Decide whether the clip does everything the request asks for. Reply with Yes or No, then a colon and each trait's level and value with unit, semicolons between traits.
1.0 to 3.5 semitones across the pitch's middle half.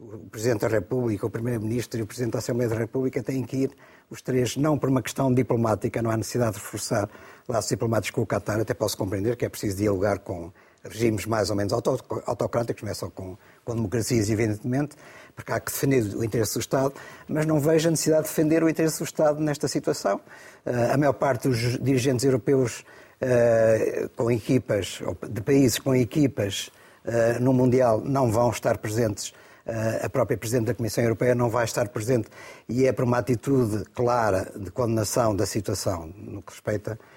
Yes: average, 3.1 semitones